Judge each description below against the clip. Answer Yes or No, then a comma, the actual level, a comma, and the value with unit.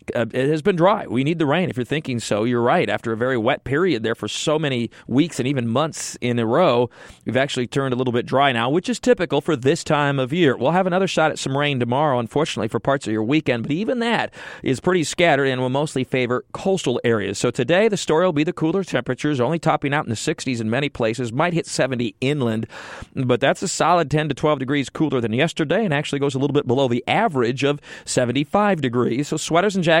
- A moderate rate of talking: No, fast, 245 wpm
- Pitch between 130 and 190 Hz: Yes, medium, 140 Hz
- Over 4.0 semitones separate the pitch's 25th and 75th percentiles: Yes, average, 4.4 semitones